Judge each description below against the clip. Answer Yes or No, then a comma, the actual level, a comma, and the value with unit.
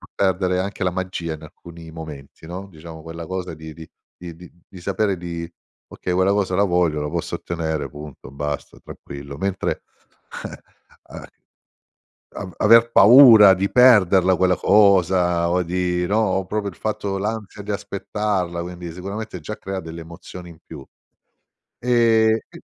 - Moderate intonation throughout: Yes, average, 3.1 semitones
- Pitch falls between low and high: No, very low, 90 Hz